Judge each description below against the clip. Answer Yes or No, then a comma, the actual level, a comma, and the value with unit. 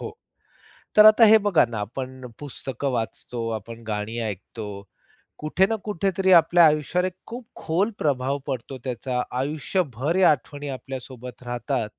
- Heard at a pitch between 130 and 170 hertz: Yes, low, 135 Hz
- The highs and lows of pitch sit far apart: Yes, wide, 6.3 semitones